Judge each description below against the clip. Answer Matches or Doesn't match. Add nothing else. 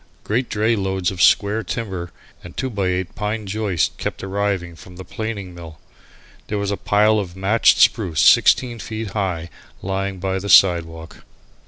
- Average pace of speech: Matches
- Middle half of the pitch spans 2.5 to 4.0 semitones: Matches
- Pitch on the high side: Doesn't match